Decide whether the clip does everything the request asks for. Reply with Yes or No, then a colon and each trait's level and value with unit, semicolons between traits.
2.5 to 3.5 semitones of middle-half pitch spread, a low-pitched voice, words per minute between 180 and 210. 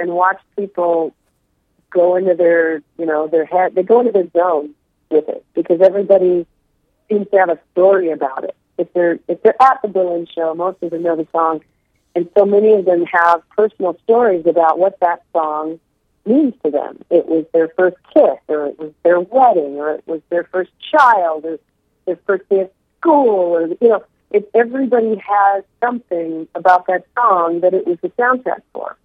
No: average, 3.2 semitones; medium, 180 Hz; average, 190 wpm